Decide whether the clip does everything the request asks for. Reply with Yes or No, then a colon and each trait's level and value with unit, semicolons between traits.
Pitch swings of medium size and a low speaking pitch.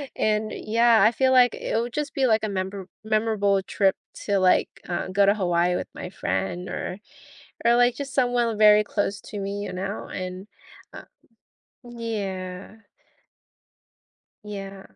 No: average, 3.1 semitones; high, 205 Hz